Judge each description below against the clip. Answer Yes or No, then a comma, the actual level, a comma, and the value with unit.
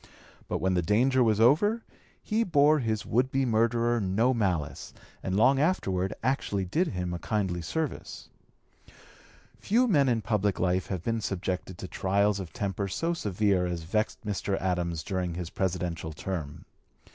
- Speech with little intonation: No, average, 5.2 semitones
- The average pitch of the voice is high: No, low, 100 Hz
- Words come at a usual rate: Yes, average, 160 wpm